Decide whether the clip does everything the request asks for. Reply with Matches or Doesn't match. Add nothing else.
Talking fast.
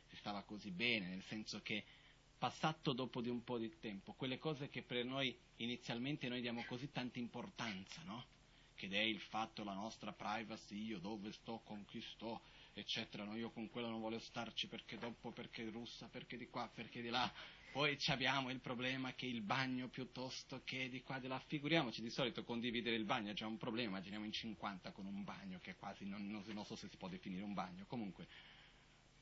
Matches